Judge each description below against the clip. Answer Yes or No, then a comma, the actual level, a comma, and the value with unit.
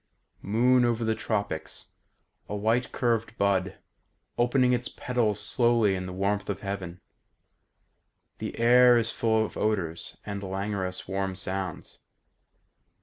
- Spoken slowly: Yes, slow, 125 wpm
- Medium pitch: No, low, 105 Hz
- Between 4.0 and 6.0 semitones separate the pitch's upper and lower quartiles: No, average, 3.5 semitones